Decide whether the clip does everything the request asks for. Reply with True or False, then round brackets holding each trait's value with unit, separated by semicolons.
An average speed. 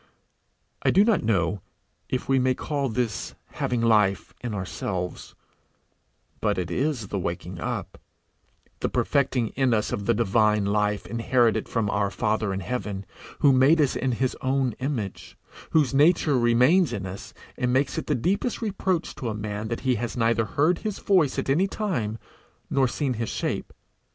True (170 wpm)